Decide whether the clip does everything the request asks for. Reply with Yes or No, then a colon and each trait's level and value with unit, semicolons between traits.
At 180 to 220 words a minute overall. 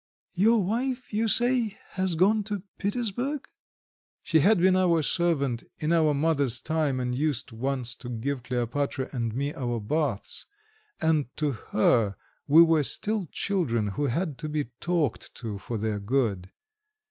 No: average, 150 wpm